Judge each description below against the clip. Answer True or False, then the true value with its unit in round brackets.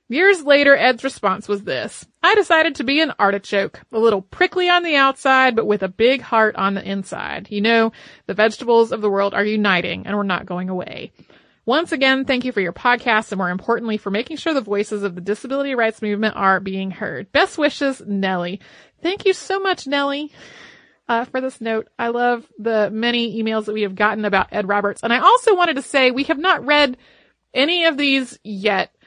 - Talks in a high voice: True (230 Hz)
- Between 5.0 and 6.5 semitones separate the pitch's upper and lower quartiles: True (5.4 semitones)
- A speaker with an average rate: False (210 wpm)